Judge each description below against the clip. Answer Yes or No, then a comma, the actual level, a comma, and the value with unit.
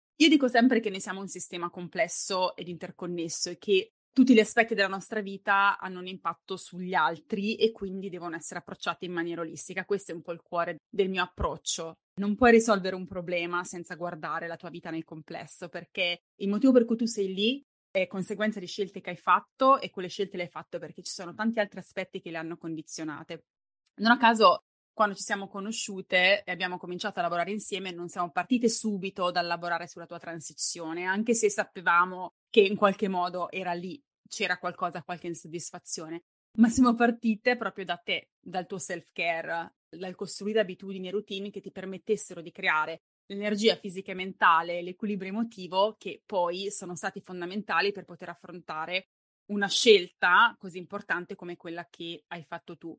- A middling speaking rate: No, fast, 185 wpm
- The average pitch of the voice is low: No, medium, 185 Hz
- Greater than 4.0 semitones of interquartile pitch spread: No, average, 2.9 semitones